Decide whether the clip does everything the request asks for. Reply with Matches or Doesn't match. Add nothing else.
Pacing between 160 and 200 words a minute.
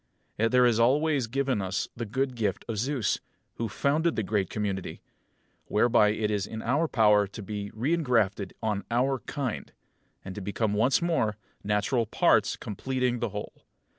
Matches